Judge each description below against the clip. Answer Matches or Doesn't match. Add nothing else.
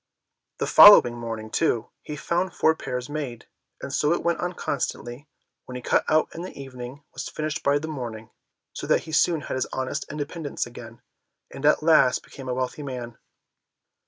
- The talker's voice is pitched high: Doesn't match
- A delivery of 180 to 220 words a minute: Matches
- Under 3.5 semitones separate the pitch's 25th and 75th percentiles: Doesn't match